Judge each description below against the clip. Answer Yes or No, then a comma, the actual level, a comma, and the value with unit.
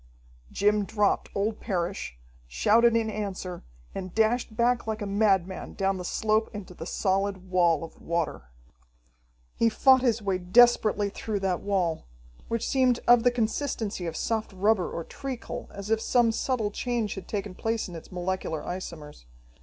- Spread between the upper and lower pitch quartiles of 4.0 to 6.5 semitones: No, average, 3.6 semitones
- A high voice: Yes, high, 205 Hz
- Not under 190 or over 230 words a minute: No, average, 160 wpm